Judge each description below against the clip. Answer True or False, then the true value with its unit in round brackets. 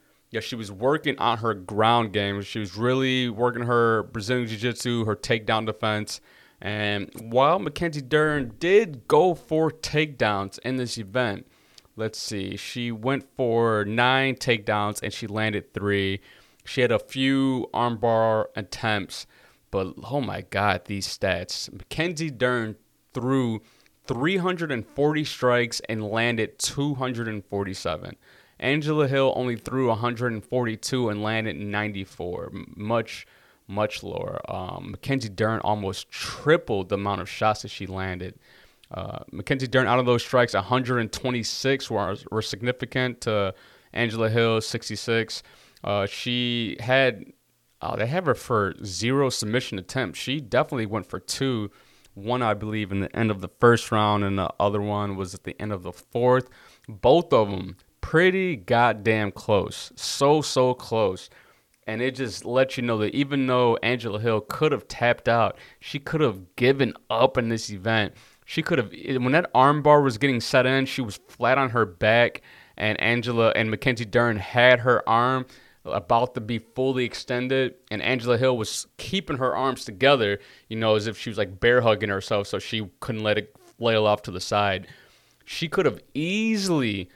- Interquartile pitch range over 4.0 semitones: False (3.6 semitones)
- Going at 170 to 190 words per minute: False (160 wpm)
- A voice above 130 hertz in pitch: False (115 Hz)